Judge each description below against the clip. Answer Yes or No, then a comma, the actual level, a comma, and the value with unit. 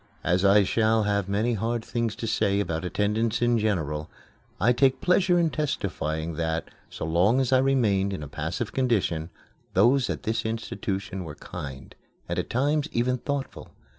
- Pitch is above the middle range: No, low, 110 Hz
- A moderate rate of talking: Yes, average, 165 wpm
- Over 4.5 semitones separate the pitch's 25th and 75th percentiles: Yes, average, 5.1 semitones